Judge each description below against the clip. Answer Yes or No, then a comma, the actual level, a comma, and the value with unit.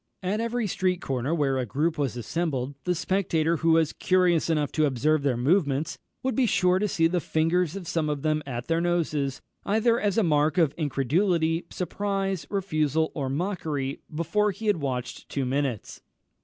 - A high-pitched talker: No, medium, 165 Hz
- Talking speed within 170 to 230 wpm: Yes, average, 180 wpm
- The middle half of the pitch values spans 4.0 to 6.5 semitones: Yes, average, 4.4 semitones